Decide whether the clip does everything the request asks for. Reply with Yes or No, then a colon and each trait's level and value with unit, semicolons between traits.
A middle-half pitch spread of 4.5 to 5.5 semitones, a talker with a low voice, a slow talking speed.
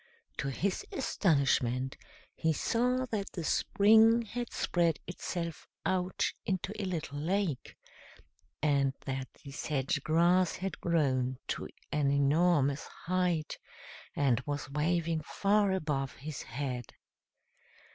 No: average, 5.1 semitones; medium, 160 Hz; slow, 115 wpm